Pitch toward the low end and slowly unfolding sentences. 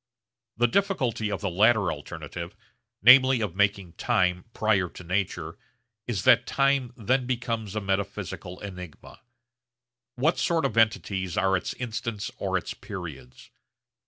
Yes: low, 100 Hz; slow, 130 wpm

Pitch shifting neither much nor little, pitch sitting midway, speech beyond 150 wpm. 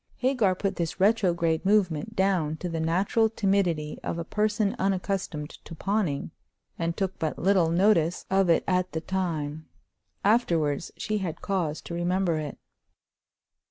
No: average, 3.4 semitones; medium, 180 Hz; average, 145 wpm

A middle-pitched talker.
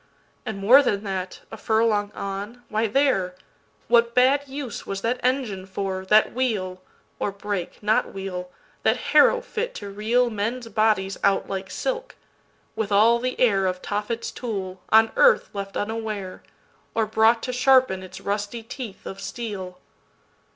No: high, 215 Hz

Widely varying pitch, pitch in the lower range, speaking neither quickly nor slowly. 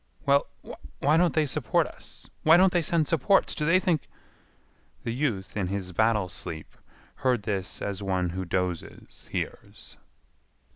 Yes: wide, 8.8 semitones; low, 115 Hz; average, 150 wpm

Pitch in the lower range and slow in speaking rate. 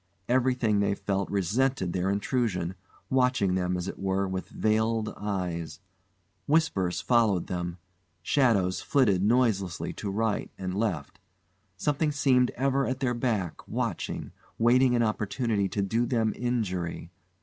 Yes: low, 105 Hz; slow, 130 wpm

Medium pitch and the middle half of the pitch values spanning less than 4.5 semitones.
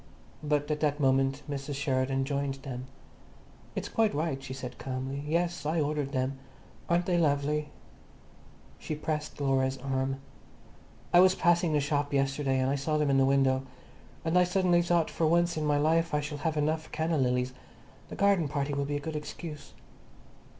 Yes: medium, 145 Hz; average, 2.8 semitones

